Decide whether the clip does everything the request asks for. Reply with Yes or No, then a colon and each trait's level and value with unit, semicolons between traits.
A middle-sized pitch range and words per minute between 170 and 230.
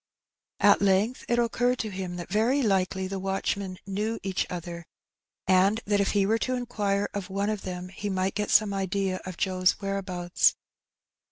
No: narrow, 2.0 semitones; average, 180 wpm